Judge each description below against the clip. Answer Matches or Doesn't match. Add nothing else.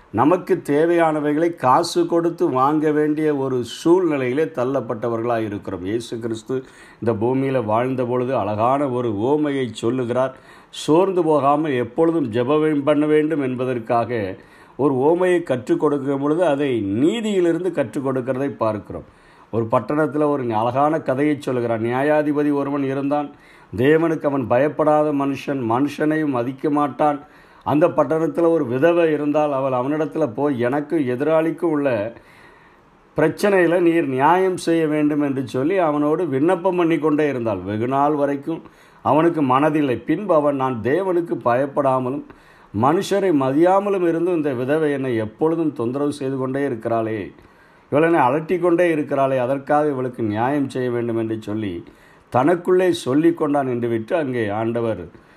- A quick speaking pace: Doesn't match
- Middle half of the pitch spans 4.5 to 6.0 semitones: Doesn't match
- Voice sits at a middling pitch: Matches